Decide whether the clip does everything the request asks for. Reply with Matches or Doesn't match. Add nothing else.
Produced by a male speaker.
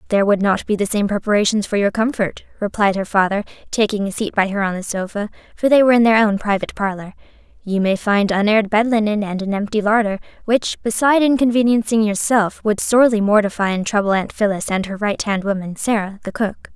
Doesn't match